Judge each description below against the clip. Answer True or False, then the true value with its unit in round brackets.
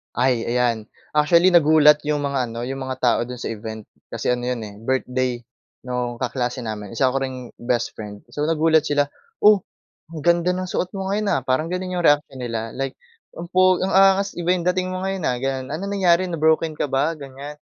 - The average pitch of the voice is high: False (145 Hz)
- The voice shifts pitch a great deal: True (5.7 semitones)